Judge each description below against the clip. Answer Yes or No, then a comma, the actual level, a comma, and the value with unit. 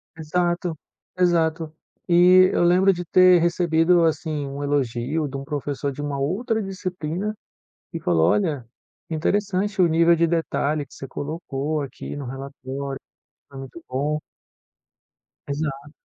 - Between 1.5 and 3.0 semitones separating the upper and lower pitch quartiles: No, average, 3.8 semitones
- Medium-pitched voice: Yes, medium, 160 Hz